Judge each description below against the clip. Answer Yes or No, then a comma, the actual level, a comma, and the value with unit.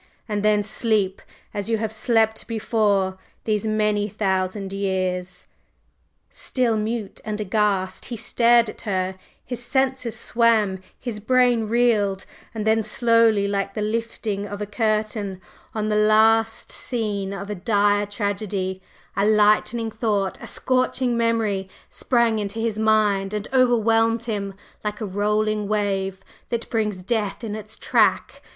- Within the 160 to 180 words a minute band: No, average, 140 wpm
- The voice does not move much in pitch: Yes, narrow, 2.1 semitones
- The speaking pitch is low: No, high, 215 Hz